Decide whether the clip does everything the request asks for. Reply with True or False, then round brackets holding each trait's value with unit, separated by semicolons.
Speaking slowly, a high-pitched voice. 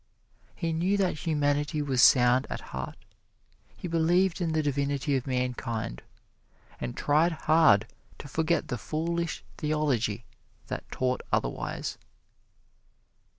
False (115 wpm; 145 Hz)